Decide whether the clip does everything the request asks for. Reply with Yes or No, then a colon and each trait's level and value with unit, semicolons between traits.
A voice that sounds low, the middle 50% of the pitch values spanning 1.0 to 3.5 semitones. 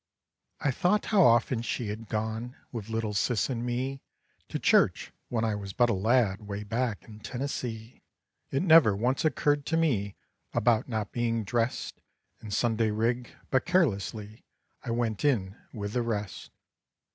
Yes: low, 115 Hz; average, 2.9 semitones